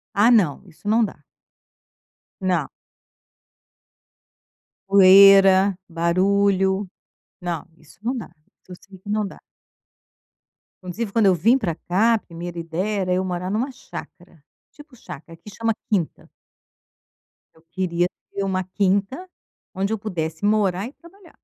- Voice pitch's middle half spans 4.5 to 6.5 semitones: No, average, 3.2 semitones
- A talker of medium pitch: No, high, 195 Hz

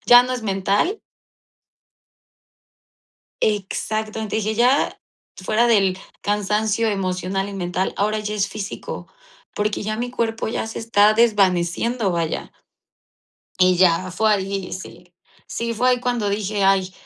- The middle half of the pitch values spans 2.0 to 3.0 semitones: Yes, narrow, 2.6 semitones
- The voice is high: Yes, high, 210 Hz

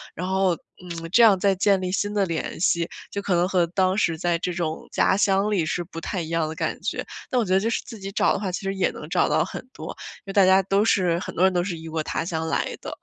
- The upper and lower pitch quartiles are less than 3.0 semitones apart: Yes, narrow, 2.6 semitones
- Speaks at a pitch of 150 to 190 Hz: Yes, medium, 185 Hz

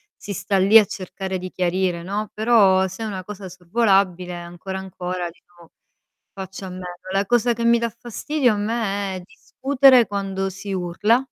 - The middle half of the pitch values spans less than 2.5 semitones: No, average, 2.8 semitones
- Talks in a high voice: Yes, high, 195 Hz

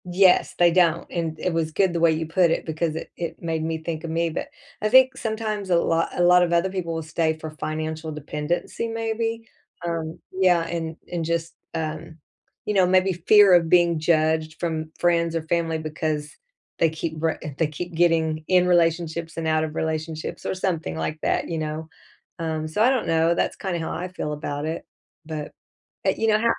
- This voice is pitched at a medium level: Yes, medium, 165 Hz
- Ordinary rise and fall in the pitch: No, narrow, 2.0 semitones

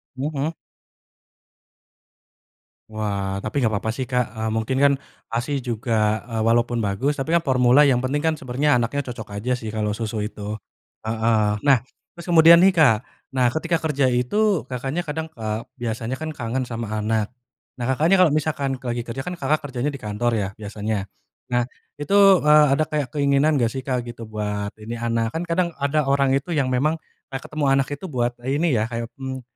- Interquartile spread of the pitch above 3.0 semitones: Yes, average, 4.2 semitones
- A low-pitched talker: Yes, low, 125 Hz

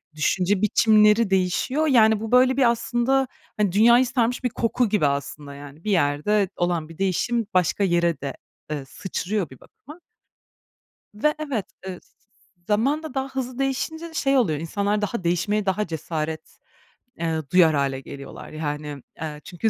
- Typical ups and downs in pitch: No, wide, 7.0 semitones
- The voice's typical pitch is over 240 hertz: No, high, 200 Hz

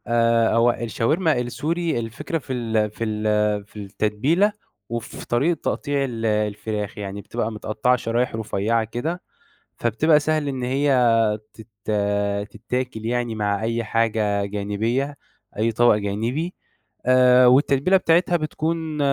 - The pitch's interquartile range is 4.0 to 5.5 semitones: Yes, average, 4.4 semitones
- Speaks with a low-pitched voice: Yes, low, 115 Hz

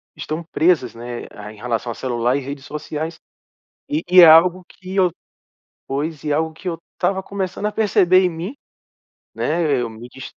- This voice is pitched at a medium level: Yes, medium, 160 Hz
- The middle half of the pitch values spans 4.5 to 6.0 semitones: Yes, wide, 5.5 semitones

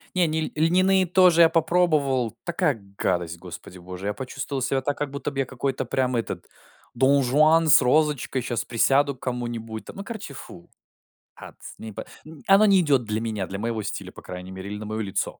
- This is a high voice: No, low, 130 Hz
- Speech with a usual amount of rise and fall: No, wide, 6.1 semitones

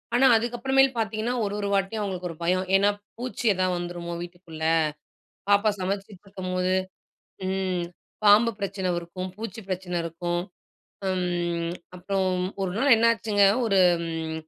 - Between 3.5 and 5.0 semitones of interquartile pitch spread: No, average, 3.1 semitones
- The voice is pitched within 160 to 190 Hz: Yes, medium, 185 Hz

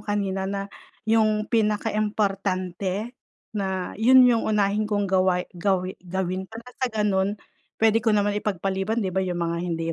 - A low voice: No, high, 200 Hz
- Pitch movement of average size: No, narrow, 2.3 semitones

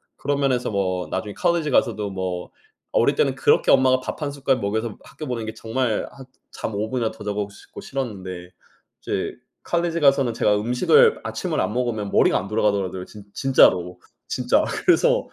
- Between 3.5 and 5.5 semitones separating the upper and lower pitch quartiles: Yes, average, 5.1 semitones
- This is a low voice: Yes, low, 115 Hz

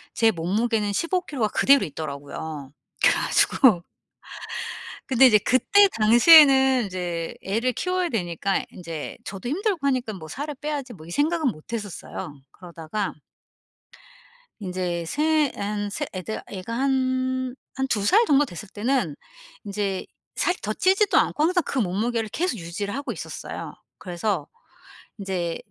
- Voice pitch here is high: Yes, high, 220 Hz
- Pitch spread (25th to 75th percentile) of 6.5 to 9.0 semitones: Yes, wide, 6.9 semitones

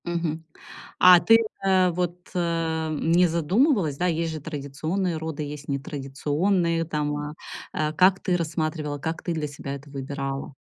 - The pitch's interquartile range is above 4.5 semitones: No, average, 2.9 semitones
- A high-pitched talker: No, medium, 160 Hz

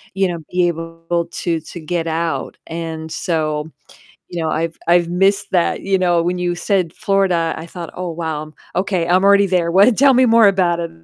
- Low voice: No, medium, 175 Hz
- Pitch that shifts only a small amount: Yes, narrow, 2.3 semitones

